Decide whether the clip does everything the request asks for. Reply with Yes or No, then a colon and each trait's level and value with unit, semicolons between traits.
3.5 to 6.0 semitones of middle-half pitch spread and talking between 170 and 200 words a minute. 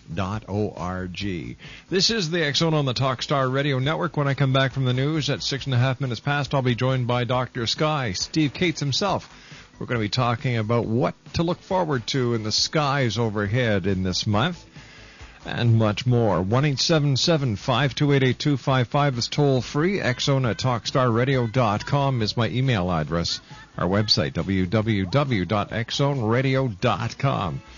No: average, 4.3 semitones; average, 155 wpm